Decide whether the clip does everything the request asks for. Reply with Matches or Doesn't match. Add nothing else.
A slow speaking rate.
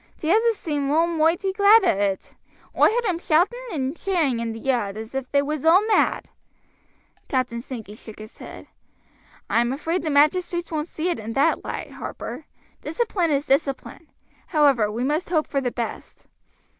Doesn't match